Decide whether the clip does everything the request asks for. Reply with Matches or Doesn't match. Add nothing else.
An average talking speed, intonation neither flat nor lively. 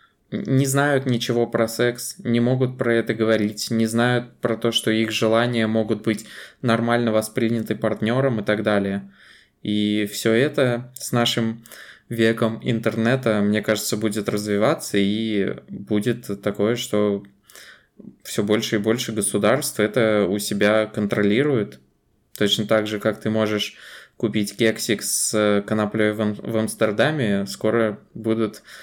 Doesn't match